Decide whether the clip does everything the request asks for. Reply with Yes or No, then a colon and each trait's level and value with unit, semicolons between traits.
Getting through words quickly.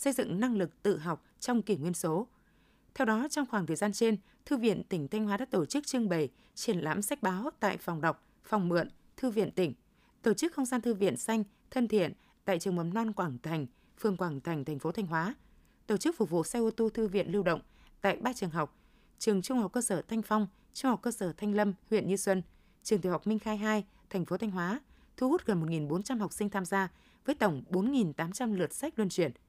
No: average, 240 wpm